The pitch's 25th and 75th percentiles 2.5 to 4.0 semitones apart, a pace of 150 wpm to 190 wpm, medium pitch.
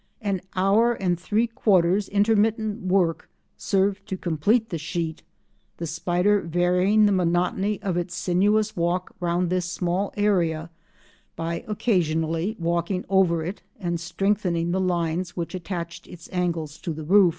No: average, 2.9 semitones; average, 140 wpm; medium, 180 Hz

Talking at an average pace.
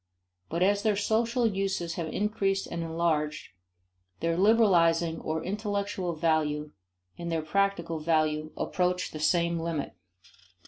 No: slow, 125 wpm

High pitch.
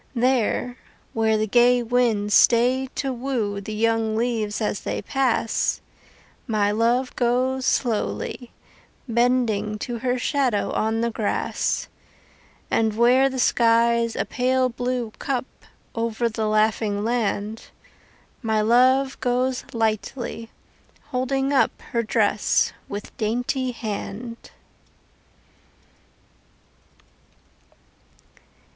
Yes: high, 235 Hz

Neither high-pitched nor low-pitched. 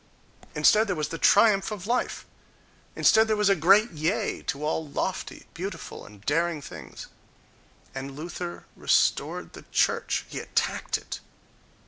Yes: medium, 175 Hz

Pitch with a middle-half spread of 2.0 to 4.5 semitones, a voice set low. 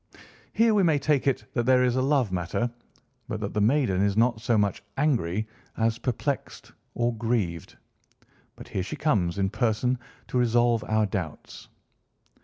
Yes: average, 4.0 semitones; low, 115 Hz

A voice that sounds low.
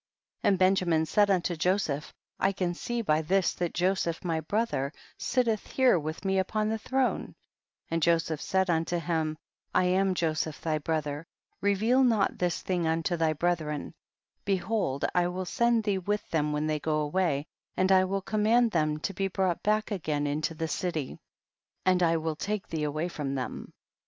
No: medium, 175 Hz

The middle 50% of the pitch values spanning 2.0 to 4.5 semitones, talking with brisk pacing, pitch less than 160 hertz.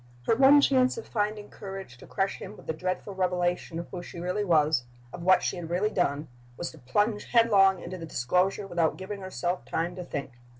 No: average, 3.4 semitones; fast, 210 wpm; medium, 185 Hz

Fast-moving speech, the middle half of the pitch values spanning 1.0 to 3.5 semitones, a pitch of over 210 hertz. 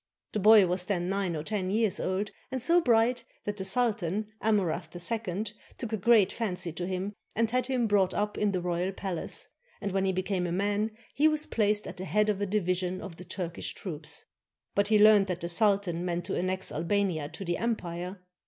No: fast, 210 wpm; average, 3.0 semitones; high, 195 Hz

